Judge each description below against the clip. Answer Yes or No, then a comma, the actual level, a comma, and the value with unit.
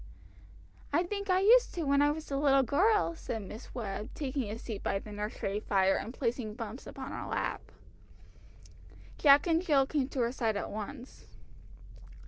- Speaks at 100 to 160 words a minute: No, average, 175 wpm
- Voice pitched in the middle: No, very high, 265 Hz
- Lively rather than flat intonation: Yes, wide, 5.9 semitones